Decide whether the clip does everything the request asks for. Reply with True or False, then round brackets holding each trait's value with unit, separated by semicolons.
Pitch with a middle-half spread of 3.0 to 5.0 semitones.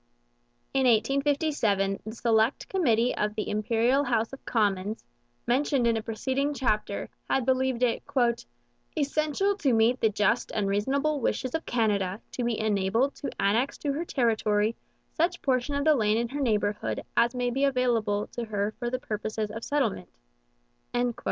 True (4.1 semitones)